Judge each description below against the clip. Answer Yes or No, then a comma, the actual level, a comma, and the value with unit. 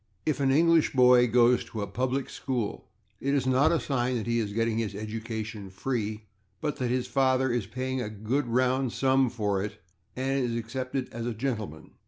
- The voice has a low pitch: Yes, low, 125 Hz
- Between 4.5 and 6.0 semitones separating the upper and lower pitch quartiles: No, average, 3.0 semitones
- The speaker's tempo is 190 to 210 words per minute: Yes, average, 195 wpm